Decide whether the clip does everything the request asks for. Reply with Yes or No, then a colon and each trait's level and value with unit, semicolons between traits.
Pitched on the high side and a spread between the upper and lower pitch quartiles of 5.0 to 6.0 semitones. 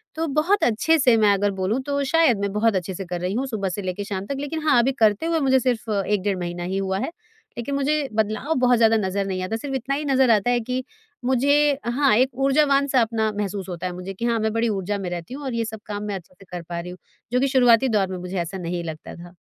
Yes: high, 220 Hz; wide, 5.6 semitones